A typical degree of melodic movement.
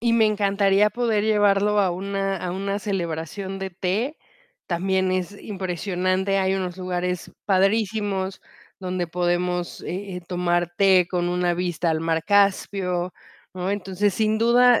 No: narrow, 2.2 semitones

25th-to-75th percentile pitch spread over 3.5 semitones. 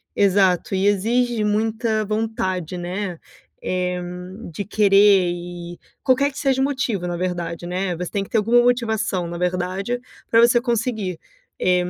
Yes: average, 4.1 semitones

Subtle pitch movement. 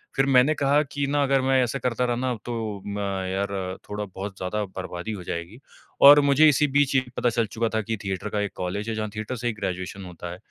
No: average, 5.3 semitones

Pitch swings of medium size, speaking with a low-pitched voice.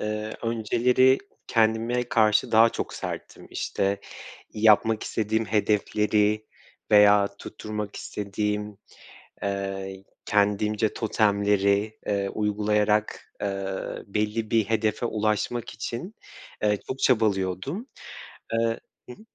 No: narrow, 1.5 semitones; low, 105 Hz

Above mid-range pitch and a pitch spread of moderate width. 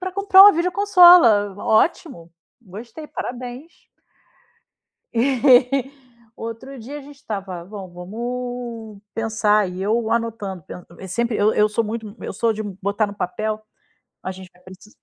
Yes: high, 225 Hz; average, 3.9 semitones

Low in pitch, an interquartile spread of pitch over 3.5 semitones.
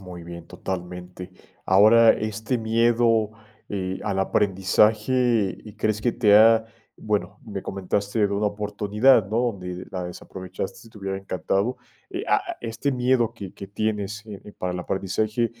No: low, 105 Hz; average, 2.7 semitones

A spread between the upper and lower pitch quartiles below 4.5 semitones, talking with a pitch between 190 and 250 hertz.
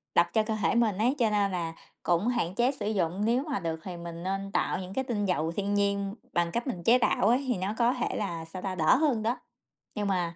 No: average, 5.0 semitones; high, 200 Hz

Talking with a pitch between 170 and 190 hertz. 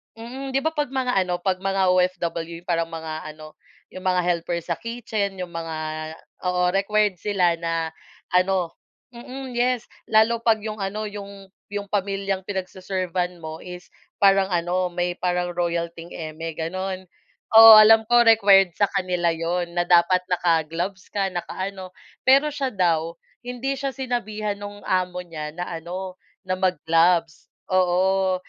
Yes: medium, 185 Hz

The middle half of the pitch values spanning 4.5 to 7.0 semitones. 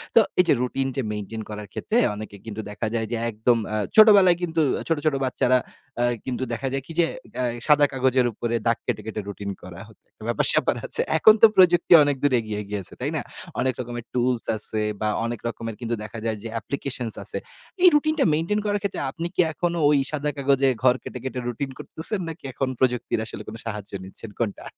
Yes: average, 5.3 semitones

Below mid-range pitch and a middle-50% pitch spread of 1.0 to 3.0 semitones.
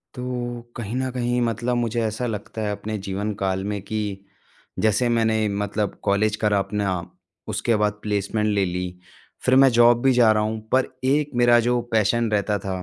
Yes: low, 110 Hz; average, 2.7 semitones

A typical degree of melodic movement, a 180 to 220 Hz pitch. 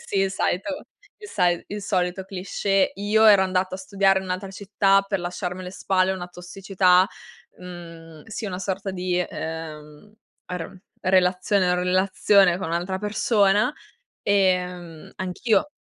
No: narrow, 1.7 semitones; medium, 185 Hz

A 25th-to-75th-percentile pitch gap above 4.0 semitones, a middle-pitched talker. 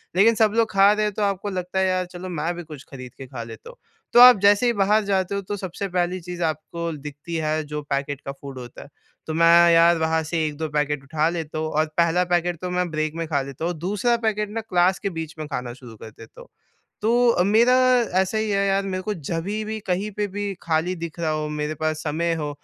Yes: average, 4.4 semitones; medium, 175 Hz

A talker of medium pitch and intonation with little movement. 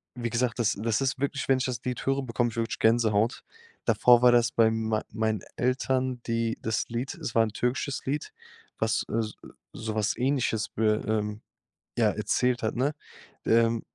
No: low, 115 Hz; narrow, 2.3 semitones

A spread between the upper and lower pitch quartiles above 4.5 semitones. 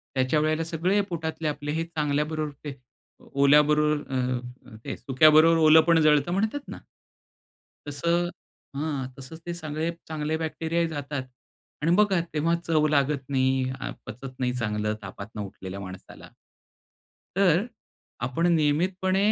No: average, 3.6 semitones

